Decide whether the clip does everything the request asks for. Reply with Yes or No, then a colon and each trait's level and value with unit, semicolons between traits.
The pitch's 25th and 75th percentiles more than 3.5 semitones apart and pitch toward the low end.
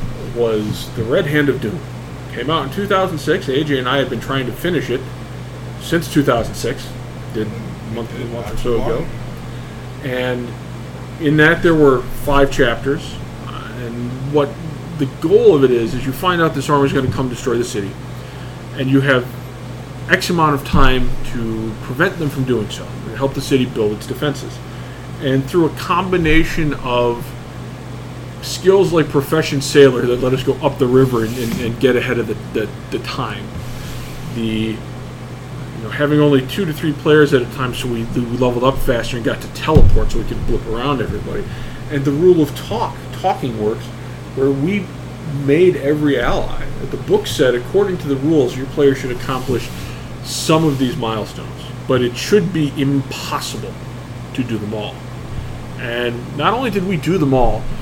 No: average, 2.8 semitones; low, 130 Hz